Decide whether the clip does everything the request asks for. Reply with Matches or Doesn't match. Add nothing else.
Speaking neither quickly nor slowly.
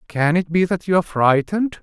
Matches